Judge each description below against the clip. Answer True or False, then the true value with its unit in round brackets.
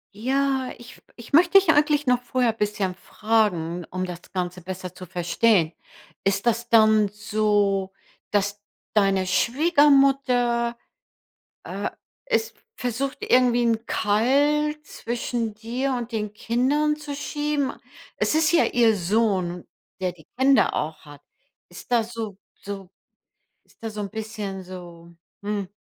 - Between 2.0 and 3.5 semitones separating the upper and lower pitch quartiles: False (5.0 semitones)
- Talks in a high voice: True (225 Hz)